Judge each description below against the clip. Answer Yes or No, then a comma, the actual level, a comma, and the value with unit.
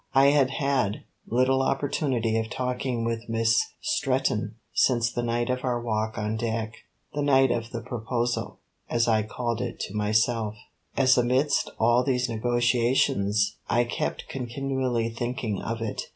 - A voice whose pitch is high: No, low, 120 Hz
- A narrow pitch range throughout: Yes, narrow, 2.3 semitones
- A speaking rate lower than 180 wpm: Yes, average, 150 wpm